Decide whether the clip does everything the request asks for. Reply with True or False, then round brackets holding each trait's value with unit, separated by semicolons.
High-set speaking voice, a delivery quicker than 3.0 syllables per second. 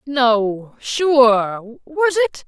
False (260 Hz; 1.8 syllables/s)